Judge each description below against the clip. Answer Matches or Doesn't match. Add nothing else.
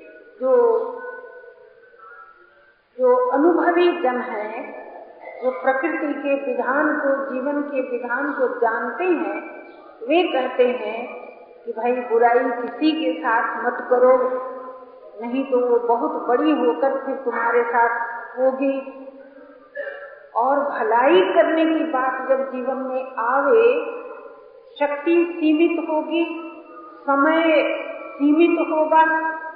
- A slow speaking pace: Matches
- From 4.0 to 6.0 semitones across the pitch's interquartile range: Matches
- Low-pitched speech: Doesn't match